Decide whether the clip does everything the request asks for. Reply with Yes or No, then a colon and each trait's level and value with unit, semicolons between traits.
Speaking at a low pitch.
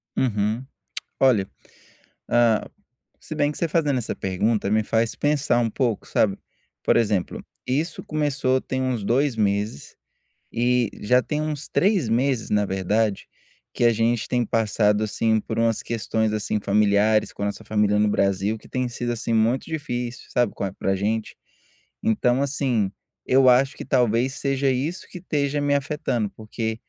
Yes: low, 115 Hz